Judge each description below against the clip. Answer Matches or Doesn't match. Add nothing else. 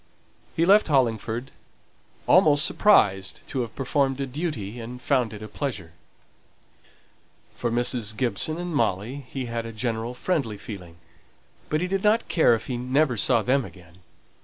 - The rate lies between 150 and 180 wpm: Matches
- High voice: Doesn't match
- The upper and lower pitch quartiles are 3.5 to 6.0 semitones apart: Matches